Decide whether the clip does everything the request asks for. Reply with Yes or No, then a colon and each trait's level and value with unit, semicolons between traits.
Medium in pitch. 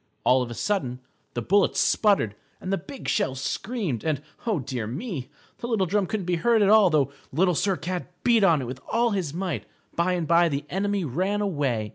Yes: medium, 180 Hz